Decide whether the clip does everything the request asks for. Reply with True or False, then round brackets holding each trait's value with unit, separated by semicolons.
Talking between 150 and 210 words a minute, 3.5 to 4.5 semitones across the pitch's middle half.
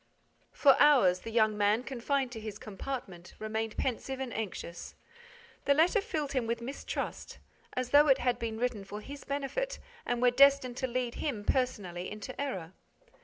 True (170 wpm; 4.2 semitones)